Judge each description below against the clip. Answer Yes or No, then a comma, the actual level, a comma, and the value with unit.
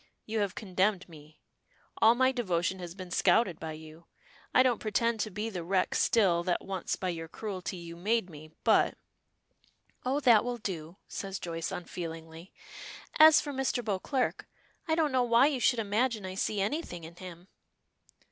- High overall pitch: Yes, high, 195 Hz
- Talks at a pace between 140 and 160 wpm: No, average, 175 wpm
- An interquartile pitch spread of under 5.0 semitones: No, wide, 5.4 semitones